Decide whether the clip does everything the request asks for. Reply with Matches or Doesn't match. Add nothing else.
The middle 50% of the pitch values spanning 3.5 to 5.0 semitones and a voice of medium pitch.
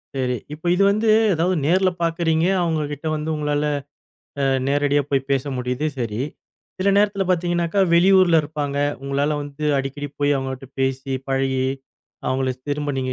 Matches